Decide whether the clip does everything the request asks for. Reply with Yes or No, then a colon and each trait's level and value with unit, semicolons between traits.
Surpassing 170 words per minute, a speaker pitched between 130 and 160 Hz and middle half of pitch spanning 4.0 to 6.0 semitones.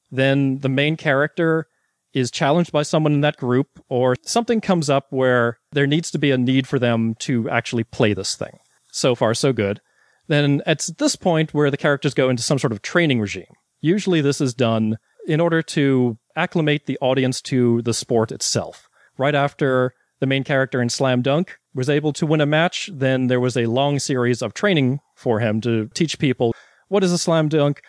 No: average, 200 wpm; medium, 140 Hz; average, 3.6 semitones